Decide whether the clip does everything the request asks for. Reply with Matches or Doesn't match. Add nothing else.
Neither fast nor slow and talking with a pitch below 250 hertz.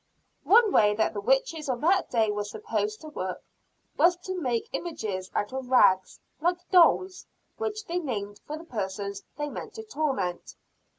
Doesn't match